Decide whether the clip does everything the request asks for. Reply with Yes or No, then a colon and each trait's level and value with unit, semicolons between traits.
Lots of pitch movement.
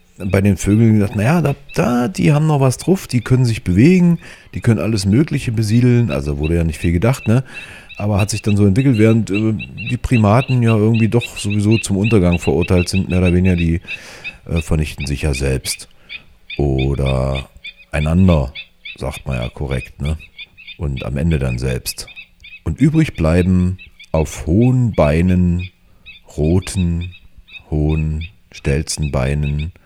Yes: wide, 6.3 semitones